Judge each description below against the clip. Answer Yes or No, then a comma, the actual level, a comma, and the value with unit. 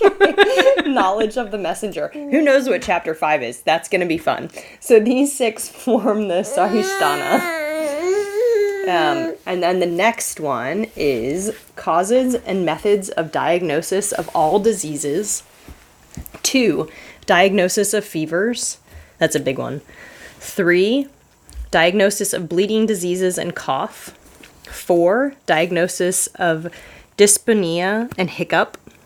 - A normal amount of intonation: No, wide, 7.0 semitones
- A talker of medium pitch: No, high, 205 Hz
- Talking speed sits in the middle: No, slow, 120 wpm